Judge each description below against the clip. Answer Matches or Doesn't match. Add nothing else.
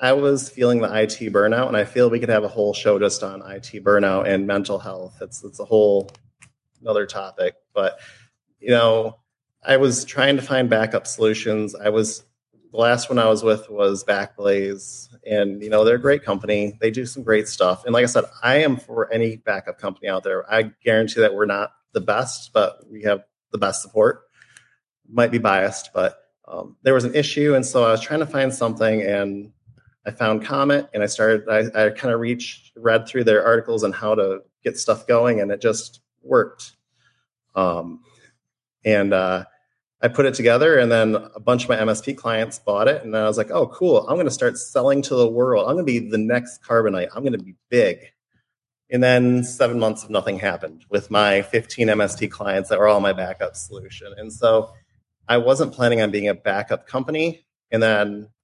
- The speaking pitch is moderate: Doesn't match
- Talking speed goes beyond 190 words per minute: Matches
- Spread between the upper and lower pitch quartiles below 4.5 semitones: Matches